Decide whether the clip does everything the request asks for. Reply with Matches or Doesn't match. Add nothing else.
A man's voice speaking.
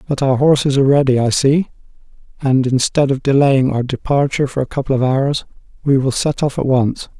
Matches